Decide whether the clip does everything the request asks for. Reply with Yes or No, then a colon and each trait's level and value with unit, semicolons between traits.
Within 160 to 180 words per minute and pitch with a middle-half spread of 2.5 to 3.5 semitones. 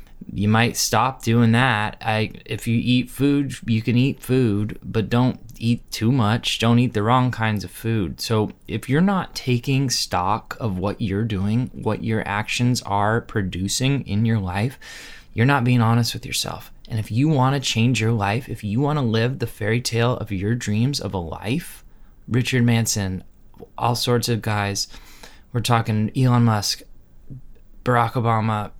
Yes: average, 175 wpm; average, 2.8 semitones